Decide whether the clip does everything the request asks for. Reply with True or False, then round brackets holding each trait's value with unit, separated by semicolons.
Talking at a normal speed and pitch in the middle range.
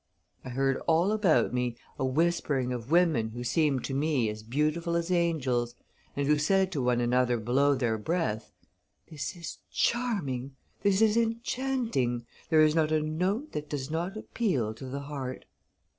True (165 wpm; 150 Hz)